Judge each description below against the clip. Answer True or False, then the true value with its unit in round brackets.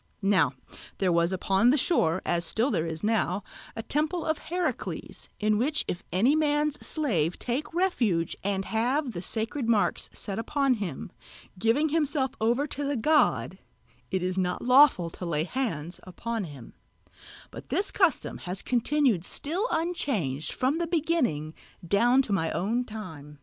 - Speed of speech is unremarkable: True (155 wpm)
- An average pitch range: False (8.1 semitones)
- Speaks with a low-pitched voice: False (230 Hz)